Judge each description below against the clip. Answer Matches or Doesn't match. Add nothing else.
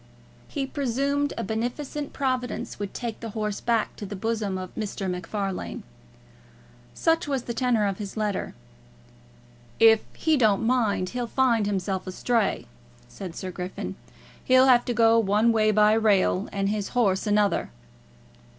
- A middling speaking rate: Matches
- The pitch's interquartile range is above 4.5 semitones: Doesn't match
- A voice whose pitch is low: Doesn't match